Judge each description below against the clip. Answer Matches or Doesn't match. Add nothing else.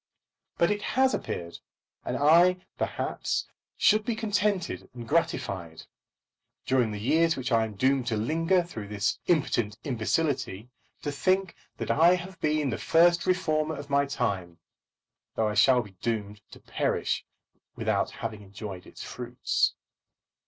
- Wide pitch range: Matches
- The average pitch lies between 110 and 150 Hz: Matches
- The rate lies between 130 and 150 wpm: Matches